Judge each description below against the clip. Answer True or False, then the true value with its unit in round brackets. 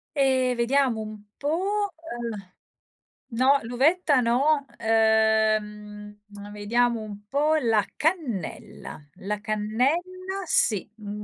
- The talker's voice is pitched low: False (235 Hz)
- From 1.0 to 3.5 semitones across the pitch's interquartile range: False (5.2 semitones)